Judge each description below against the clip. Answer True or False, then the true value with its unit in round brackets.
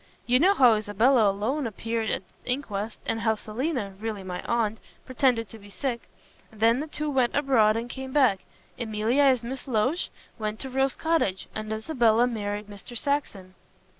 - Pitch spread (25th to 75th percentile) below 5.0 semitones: True (3.8 semitones)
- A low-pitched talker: False (230 Hz)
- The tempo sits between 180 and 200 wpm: False (170 wpm)